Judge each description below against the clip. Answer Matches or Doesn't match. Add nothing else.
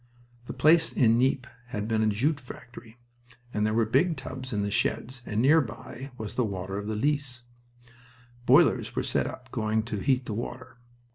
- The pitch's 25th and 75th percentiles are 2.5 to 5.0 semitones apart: Matches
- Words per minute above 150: Matches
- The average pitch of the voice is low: Matches